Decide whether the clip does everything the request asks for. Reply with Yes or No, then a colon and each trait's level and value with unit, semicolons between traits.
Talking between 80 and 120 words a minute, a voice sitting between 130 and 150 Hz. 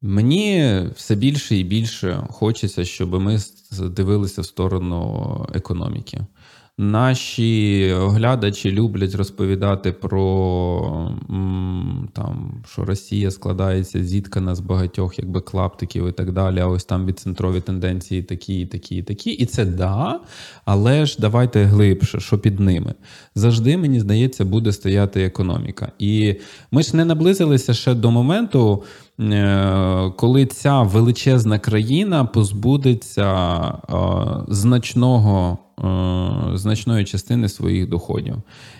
No: average, 110 wpm; low, 105 Hz